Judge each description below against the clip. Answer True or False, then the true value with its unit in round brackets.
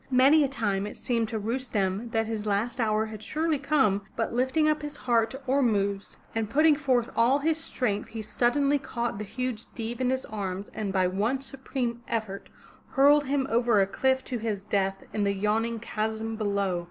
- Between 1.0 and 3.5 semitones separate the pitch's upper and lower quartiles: False (4.0 semitones)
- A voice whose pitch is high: True (230 Hz)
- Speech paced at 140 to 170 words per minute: False (190 wpm)